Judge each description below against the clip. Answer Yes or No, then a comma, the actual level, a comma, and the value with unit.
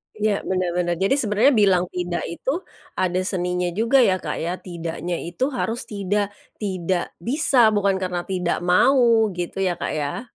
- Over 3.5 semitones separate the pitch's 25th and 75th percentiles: Yes, average, 3.9 semitones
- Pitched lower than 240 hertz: Yes, high, 190 Hz